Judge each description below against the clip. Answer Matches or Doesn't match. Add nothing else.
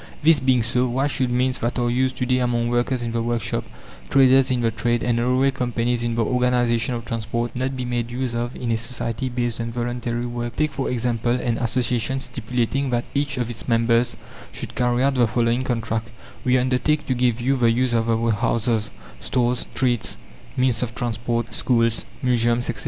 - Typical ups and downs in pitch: Doesn't match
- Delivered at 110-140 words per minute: Doesn't match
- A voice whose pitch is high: Doesn't match